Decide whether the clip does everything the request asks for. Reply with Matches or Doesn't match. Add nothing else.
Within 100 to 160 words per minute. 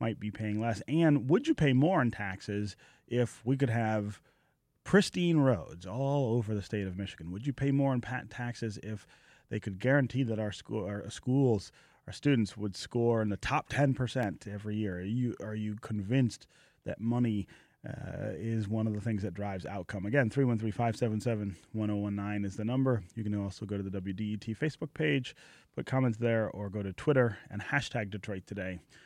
Doesn't match